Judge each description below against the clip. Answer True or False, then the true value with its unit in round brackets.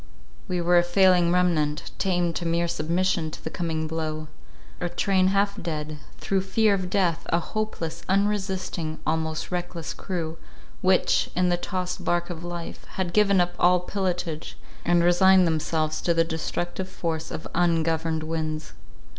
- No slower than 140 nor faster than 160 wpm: True (150 wpm)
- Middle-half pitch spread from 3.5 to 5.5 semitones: False (2.4 semitones)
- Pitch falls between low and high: True (175 Hz)